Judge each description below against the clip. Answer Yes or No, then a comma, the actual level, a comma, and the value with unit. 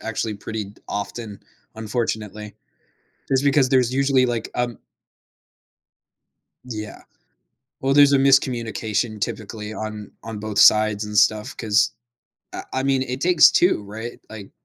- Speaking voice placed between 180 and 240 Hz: No, low, 110 Hz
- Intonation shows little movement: No, average, 3.5 semitones